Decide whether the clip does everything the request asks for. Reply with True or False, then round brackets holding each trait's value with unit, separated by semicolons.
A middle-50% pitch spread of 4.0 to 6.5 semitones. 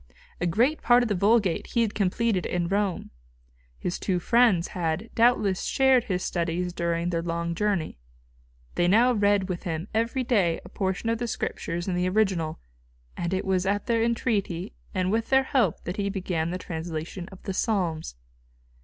True (4.4 semitones)